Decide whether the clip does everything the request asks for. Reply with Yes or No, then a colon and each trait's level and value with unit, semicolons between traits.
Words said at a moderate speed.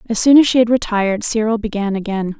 No: fast, 225 wpm